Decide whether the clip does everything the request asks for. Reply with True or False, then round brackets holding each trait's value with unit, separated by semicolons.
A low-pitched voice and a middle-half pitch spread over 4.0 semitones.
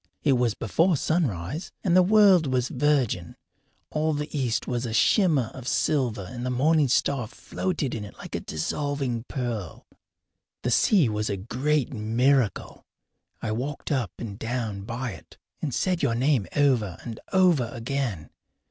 True (125 Hz; 4.7 semitones)